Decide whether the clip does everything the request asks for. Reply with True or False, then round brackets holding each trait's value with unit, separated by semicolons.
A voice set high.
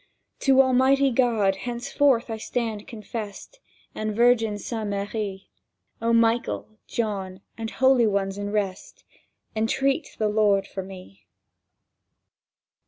True (220 Hz)